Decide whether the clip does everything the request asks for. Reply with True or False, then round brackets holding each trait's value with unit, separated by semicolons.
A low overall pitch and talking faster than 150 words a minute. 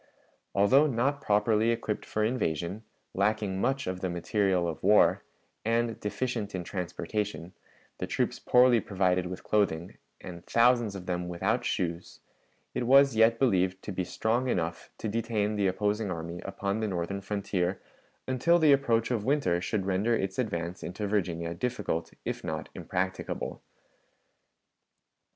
False (100 Hz; 145 wpm)